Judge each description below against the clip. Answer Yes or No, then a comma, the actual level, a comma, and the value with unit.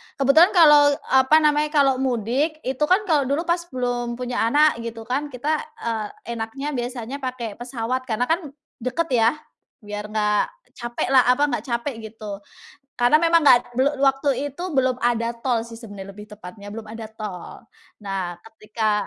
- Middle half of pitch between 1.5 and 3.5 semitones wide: No, average, 4.1 semitones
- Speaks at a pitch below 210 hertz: No, high, 245 Hz